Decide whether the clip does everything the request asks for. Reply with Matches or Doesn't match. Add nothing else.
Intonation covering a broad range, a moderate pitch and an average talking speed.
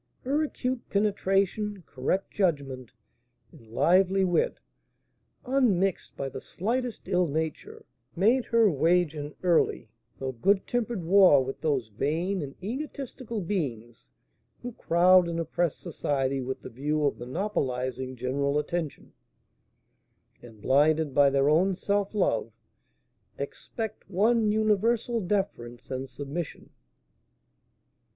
Doesn't match